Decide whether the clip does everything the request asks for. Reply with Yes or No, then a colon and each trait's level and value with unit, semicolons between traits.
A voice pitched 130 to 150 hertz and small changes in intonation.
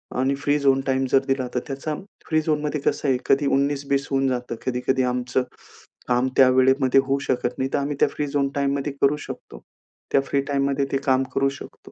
Yes: low, 135 Hz; narrow, 1.3 semitones